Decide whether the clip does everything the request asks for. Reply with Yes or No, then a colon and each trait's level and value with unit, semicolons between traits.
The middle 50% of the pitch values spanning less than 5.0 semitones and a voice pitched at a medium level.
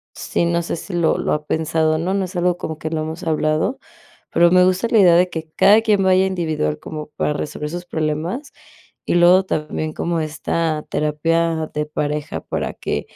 Yes: narrow, 2.6 semitones; medium, 165 Hz